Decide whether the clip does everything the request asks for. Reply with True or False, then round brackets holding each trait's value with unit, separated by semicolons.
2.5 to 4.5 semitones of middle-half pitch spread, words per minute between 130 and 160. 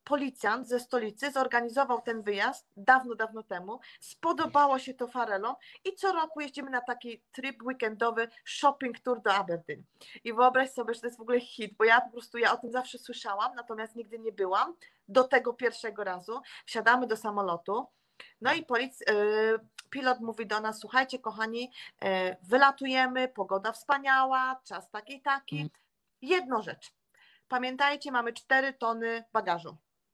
True (2.9 semitones; 150 wpm)